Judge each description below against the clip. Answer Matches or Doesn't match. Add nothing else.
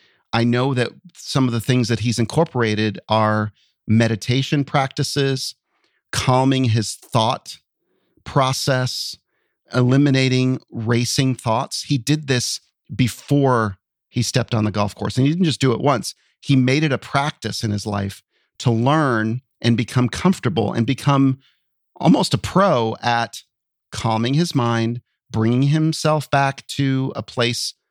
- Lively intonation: Doesn't match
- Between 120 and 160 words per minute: Matches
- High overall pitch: Doesn't match